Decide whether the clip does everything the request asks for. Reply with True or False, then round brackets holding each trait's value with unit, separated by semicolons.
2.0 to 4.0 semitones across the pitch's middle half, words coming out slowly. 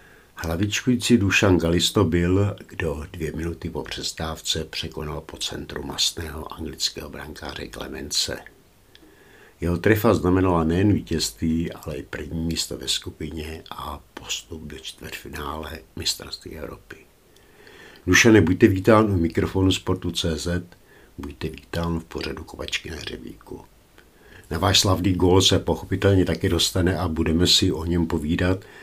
False (2.7 semitones; 125 wpm)